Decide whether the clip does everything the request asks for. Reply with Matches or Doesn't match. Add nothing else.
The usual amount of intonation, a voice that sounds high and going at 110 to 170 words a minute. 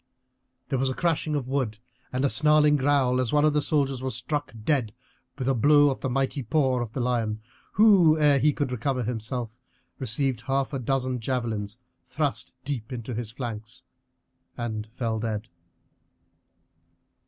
Doesn't match